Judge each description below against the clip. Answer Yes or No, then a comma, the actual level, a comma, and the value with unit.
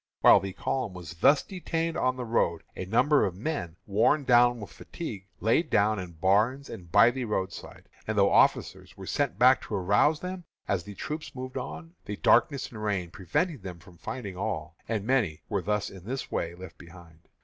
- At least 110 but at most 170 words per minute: No, average, 195 wpm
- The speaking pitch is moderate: No, low, 105 Hz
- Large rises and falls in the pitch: Yes, wide, 5.9 semitones